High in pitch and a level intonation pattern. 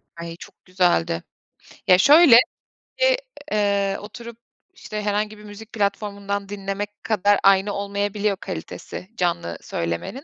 Yes: high, 200 Hz; narrow, 1.7 semitones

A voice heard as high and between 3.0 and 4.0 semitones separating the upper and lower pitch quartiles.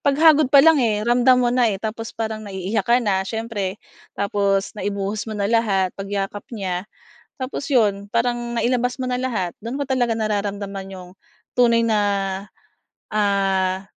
Yes: high, 215 Hz; average, 3.4 semitones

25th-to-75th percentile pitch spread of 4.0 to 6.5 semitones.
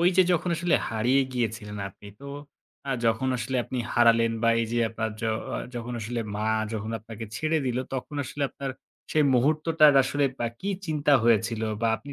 Yes: average, 4.3 semitones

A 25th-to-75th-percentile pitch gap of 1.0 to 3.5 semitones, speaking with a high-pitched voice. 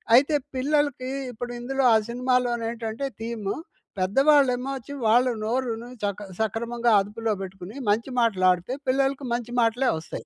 Yes: average, 2.8 semitones; high, 240 Hz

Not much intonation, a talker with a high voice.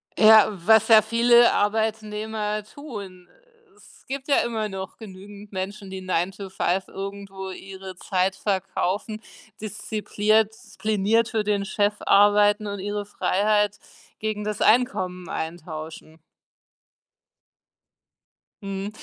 Yes: narrow, 2.1 semitones; high, 205 Hz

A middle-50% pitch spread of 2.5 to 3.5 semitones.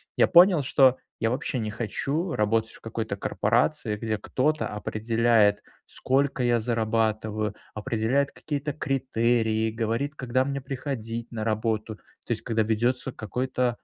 Yes: average, 3.2 semitones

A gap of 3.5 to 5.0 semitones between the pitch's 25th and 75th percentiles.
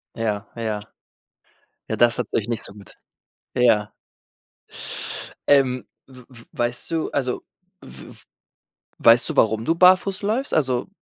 Yes: average, 4.1 semitones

